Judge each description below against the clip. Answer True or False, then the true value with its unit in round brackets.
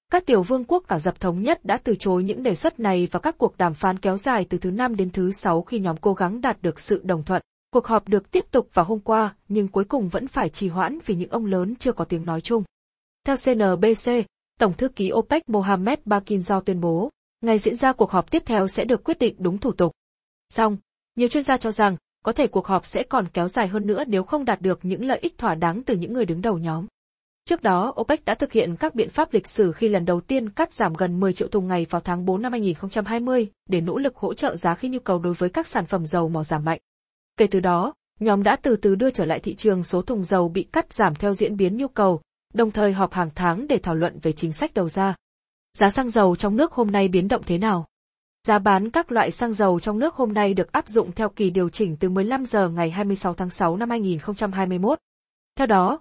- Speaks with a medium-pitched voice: False (205 Hz)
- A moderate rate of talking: False (255 wpm)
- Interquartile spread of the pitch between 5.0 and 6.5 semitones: False (4.3 semitones)